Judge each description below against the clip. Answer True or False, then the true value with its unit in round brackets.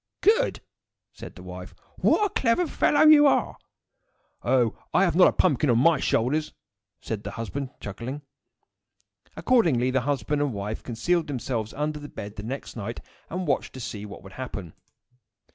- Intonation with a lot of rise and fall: True (6.6 semitones)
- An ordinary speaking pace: True (165 wpm)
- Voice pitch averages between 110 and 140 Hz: True (135 Hz)